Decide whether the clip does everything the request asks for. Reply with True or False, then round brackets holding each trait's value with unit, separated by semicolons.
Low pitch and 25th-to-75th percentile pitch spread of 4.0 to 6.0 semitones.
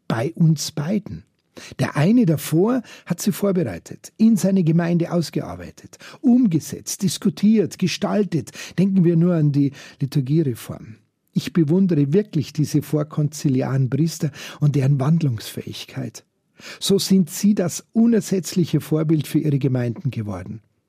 False (160 Hz; 4.8 semitones)